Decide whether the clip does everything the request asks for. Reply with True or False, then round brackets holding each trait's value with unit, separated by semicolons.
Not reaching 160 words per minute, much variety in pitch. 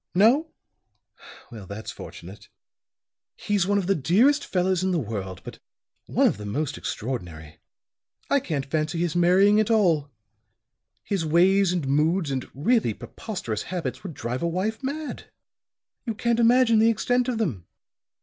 True (150 wpm; 8.2 semitones)